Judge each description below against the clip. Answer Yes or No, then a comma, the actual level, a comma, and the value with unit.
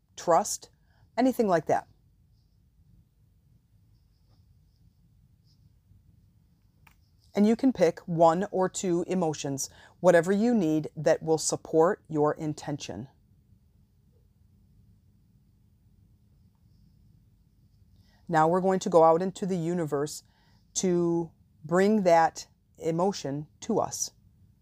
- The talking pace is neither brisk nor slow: No, slow, 85 wpm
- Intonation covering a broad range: Yes, wide, 9.0 semitones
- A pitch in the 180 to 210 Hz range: No, medium, 150 Hz